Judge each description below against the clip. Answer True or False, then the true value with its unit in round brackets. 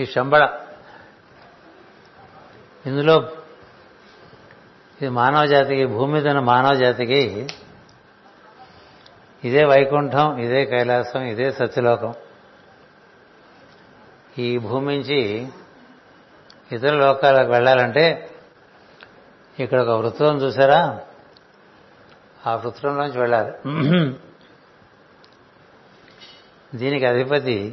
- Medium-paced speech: False (65 wpm)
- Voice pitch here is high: False (135 Hz)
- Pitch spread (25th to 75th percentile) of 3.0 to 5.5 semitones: False (2.6 semitones)